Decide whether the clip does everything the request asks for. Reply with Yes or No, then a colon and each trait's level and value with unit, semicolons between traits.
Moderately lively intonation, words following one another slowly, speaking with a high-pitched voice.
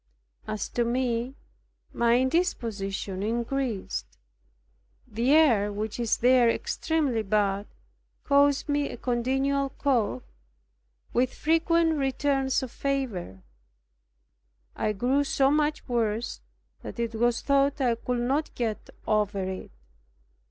Yes: average, 4.1 semitones; slow, 110 wpm; high, 245 Hz